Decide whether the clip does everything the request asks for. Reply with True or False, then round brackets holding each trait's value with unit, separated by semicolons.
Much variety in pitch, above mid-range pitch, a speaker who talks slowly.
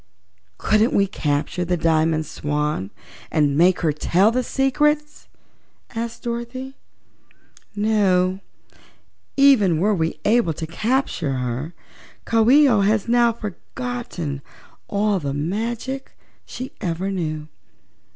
True (6.7 semitones; 200 Hz; 110 wpm)